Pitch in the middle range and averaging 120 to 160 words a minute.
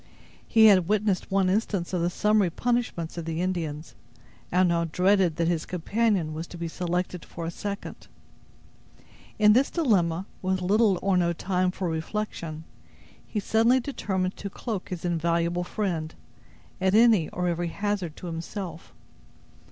Yes: medium, 180 Hz; average, 150 wpm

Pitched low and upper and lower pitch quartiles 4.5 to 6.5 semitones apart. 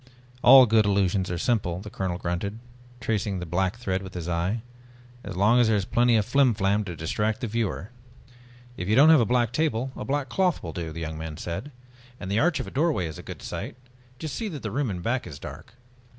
Yes: low, 105 Hz; average, 5.3 semitones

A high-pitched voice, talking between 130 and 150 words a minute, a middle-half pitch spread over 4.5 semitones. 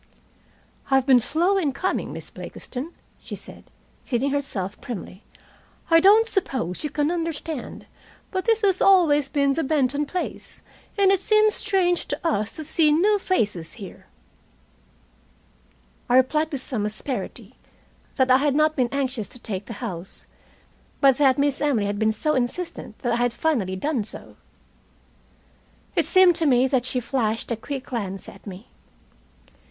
No: very high, 275 Hz; average, 160 wpm; wide, 5.4 semitones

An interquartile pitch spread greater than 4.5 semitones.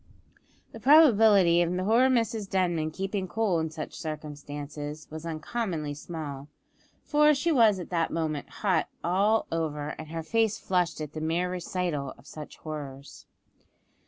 Yes: average, 5.2 semitones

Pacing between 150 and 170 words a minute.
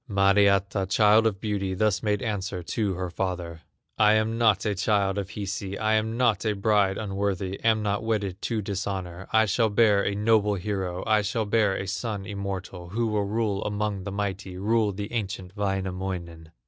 No: average, 180 wpm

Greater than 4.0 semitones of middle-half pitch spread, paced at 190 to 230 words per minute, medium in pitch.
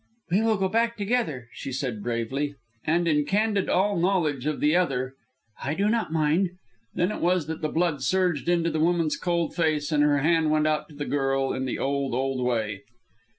Yes: average, 4.5 semitones; average, 200 wpm; medium, 155 Hz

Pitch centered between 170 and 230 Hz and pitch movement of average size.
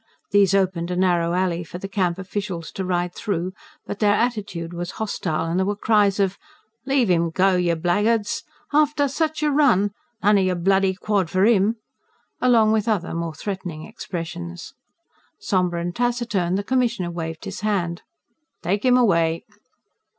Yes: high, 190 Hz; average, 3.5 semitones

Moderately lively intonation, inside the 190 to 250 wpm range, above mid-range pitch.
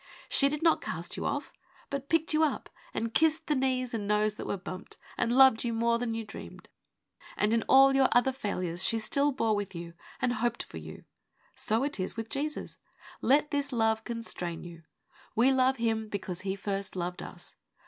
Yes: average, 4.5 semitones; average, 200 wpm; high, 230 Hz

